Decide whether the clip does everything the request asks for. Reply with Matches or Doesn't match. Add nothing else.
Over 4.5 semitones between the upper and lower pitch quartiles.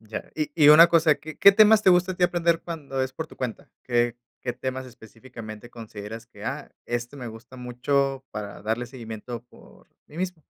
Matches